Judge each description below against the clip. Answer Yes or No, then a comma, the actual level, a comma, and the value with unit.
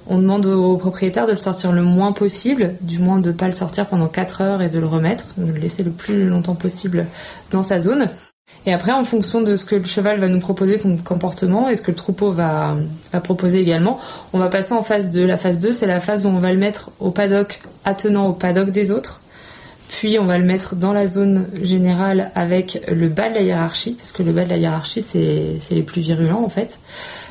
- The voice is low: No, medium, 185 Hz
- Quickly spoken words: Yes, fast, 240 wpm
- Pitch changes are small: Yes, narrow, 2.3 semitones